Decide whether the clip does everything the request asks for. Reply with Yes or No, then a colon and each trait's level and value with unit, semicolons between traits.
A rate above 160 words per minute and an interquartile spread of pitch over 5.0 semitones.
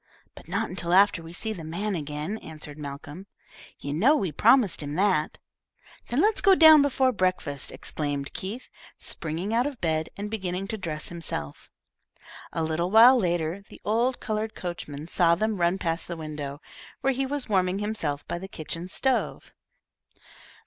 Yes: average, 170 wpm; wide, 5.6 semitones